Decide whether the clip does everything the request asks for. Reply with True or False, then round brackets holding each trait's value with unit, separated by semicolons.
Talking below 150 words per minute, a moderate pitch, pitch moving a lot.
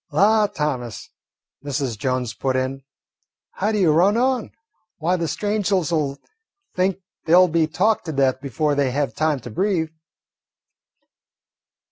True (140 wpm; 155 Hz; 5.8 semitones)